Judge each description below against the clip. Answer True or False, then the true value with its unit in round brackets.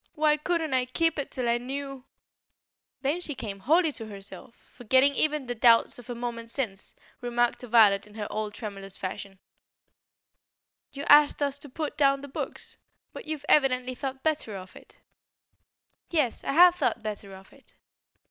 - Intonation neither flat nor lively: True (4.7 semitones)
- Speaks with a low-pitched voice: False (255 Hz)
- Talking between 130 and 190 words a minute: True (175 wpm)